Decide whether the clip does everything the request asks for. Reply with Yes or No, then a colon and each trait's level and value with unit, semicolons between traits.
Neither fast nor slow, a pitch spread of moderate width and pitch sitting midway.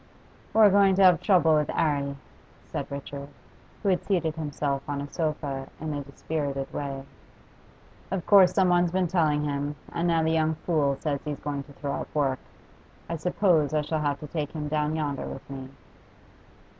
Yes: average, 180 wpm; average, 3.0 semitones; medium, 150 Hz